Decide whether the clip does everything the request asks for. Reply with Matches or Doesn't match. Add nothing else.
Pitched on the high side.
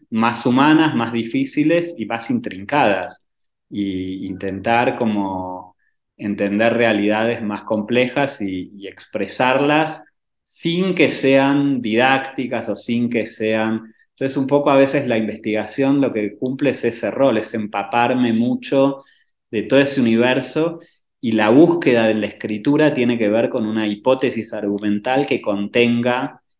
Doesn't match